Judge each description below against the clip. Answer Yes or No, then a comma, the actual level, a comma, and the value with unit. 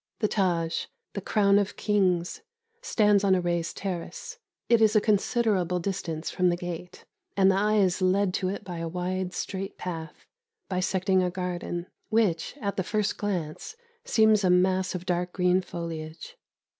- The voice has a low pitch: No, medium, 185 Hz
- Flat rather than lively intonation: Yes, narrow, 2.3 semitones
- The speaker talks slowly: No, average, 165 wpm